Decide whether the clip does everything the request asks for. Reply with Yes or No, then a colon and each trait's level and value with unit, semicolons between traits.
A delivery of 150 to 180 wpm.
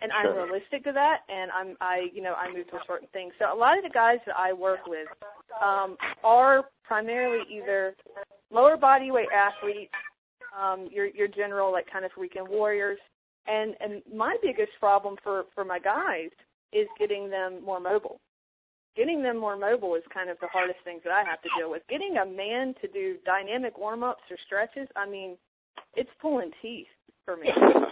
No: average, 195 wpm